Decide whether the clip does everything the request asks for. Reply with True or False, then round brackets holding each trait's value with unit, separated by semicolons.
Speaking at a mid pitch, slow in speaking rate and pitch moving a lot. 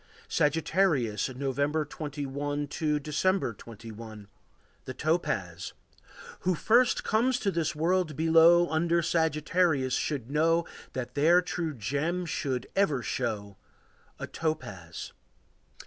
False (150 Hz; 105 wpm; 4.6 semitones)